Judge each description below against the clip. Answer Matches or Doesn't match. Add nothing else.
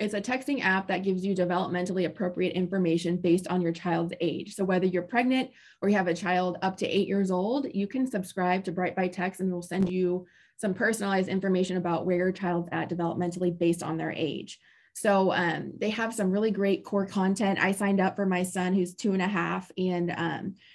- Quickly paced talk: Matches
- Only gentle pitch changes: Matches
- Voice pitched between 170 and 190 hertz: Matches